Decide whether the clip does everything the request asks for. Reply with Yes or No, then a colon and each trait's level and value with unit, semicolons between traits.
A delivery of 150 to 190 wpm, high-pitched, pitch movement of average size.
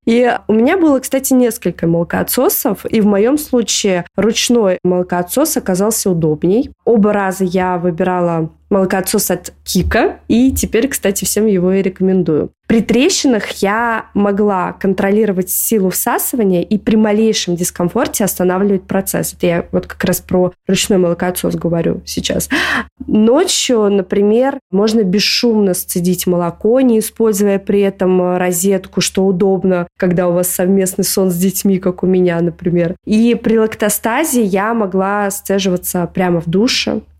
No: average, 135 wpm; high, 195 Hz; average, 3.5 semitones